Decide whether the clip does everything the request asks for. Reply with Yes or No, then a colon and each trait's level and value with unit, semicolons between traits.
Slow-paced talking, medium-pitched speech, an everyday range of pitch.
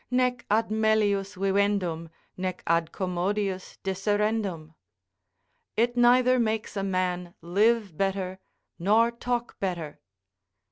No: slow, 100 wpm; high, 200 Hz; average, 3.3 semitones